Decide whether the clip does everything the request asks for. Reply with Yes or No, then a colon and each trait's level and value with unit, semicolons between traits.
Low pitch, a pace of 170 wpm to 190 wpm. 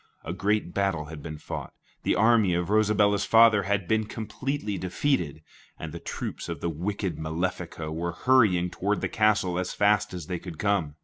Yes: very low, 95 Hz; average, 180 wpm